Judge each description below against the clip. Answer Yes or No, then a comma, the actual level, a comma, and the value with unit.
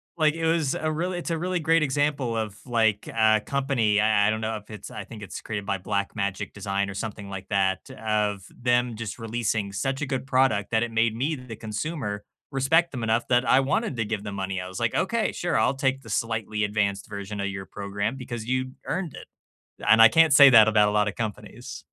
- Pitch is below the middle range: Yes, low, 110 Hz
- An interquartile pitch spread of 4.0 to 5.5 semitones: Yes, average, 4.6 semitones